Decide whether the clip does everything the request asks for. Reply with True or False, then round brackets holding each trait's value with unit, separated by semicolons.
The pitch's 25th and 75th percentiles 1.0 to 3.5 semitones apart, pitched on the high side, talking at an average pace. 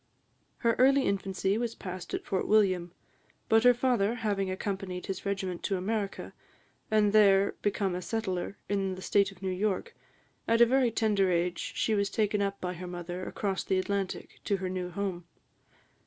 True (2.5 semitones; 195 Hz; 170 wpm)